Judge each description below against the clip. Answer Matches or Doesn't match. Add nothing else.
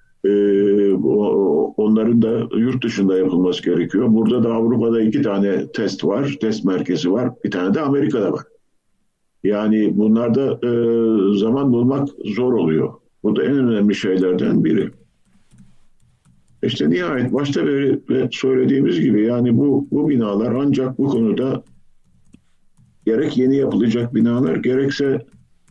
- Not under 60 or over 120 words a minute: Matches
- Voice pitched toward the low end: Matches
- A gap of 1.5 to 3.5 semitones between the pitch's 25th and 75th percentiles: Doesn't match